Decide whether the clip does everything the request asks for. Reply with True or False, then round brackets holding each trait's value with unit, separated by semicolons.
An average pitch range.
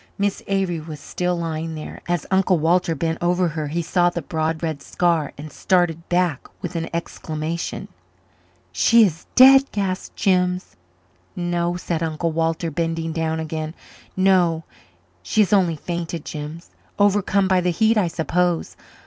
False (2.1 semitones)